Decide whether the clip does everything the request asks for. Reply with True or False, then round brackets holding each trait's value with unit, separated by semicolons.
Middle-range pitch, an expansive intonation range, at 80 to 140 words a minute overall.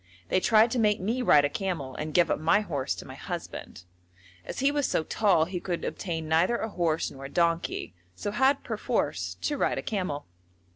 False (180 Hz; 5.8 semitones; 205 wpm)